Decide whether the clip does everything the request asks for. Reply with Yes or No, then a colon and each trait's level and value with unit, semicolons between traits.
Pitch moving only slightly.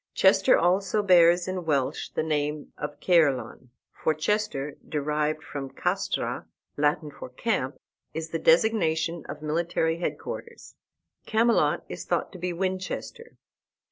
No: average, 3.8 semitones